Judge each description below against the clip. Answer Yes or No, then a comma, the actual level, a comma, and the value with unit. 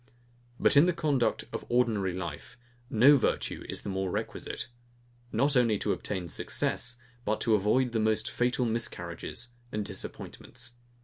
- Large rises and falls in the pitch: No, average, 3.4 semitones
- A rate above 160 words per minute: No, average, 140 wpm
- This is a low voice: Yes, low, 115 Hz